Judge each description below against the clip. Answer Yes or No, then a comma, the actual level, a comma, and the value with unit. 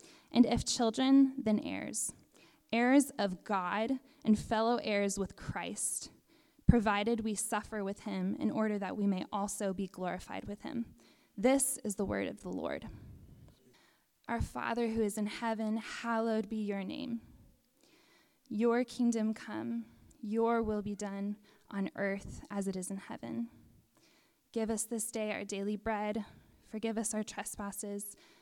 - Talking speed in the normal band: Yes, average, 150 wpm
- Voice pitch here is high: Yes, high, 215 Hz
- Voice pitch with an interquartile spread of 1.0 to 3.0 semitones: Yes, average, 2.7 semitones